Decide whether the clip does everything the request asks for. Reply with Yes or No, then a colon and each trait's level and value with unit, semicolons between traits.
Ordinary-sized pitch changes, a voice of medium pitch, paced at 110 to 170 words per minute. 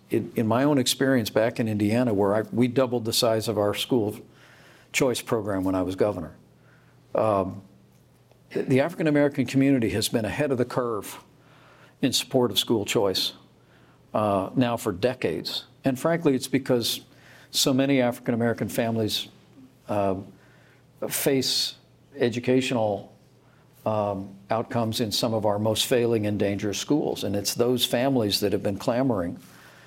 No: average, 4.1 semitones; low, 120 Hz; average, 145 wpm